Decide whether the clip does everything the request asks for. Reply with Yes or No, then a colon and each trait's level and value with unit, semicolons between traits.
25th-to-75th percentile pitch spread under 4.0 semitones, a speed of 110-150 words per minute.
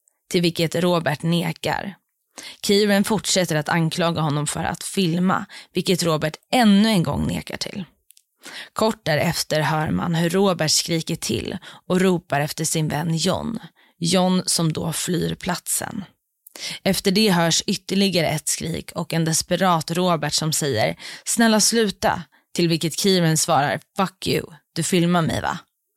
Yes: average, 3.1 semitones; average, 145 wpm